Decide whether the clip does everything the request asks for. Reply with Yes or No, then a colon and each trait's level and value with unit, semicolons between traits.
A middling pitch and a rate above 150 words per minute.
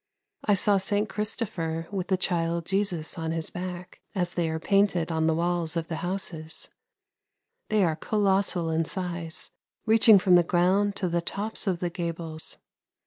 Yes: medium, 175 Hz; average, 165 wpm